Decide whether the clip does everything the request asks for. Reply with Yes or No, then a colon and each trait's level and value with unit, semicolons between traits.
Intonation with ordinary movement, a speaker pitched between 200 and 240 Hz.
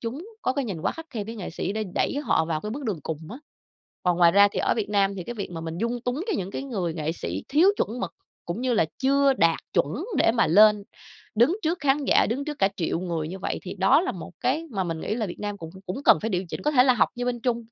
No: wide, 6.2 semitones; high, 210 Hz